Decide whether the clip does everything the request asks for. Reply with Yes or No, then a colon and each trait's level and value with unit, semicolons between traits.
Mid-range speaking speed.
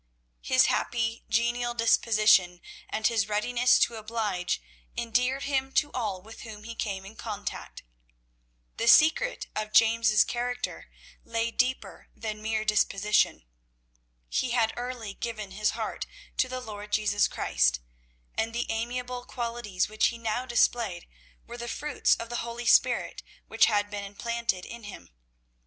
Yes: average, 145 wpm